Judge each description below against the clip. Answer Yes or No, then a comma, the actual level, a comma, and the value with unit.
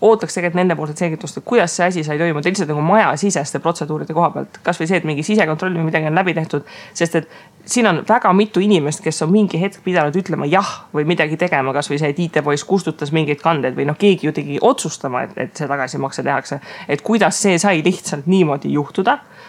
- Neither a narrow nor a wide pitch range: Yes, average, 3.7 semitones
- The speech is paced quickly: Yes, fast, 210 wpm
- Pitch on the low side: No, medium, 170 Hz